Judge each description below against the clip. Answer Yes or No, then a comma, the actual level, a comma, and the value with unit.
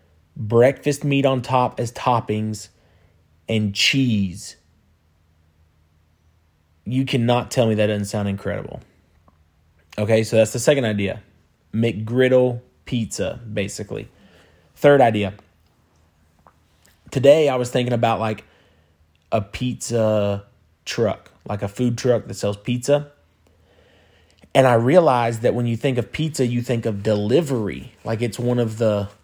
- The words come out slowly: Yes, slow, 125 wpm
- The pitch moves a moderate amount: No, wide, 6.4 semitones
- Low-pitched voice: Yes, low, 105 Hz